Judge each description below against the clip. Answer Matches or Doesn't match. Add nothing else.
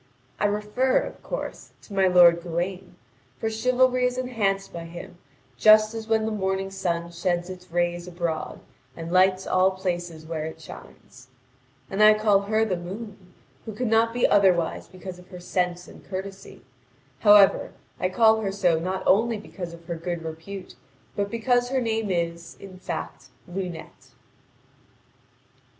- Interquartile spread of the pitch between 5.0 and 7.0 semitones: Doesn't match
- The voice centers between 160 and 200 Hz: Matches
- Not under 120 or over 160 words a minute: Matches